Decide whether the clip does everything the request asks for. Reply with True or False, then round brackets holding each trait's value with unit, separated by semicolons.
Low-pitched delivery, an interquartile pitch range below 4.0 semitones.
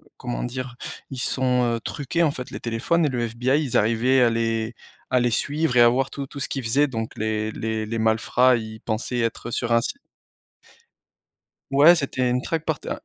True (125 Hz; 2.9 semitones)